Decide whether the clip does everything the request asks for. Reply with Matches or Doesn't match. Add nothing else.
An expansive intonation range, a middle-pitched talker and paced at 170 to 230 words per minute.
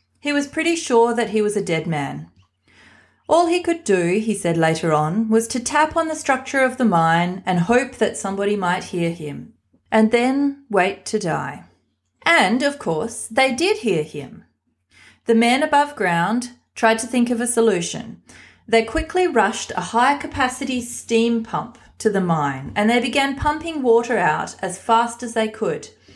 Doesn't match